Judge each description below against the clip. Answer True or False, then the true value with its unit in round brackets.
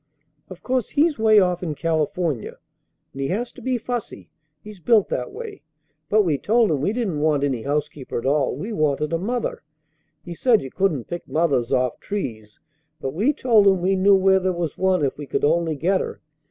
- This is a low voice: False (175 Hz)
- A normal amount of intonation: False (6.0 semitones)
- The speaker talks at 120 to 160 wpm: False (205 wpm)